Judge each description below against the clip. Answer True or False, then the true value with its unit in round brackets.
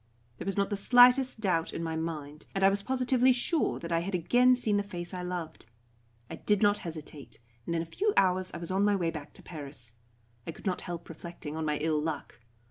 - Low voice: False (180 Hz)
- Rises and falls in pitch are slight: False (4.2 semitones)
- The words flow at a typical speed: False (230 wpm)